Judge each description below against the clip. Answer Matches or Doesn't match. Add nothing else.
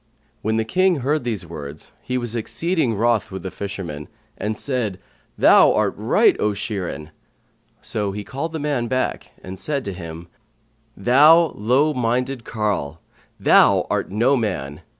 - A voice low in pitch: Matches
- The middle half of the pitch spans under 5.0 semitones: Doesn't match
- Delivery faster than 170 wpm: Doesn't match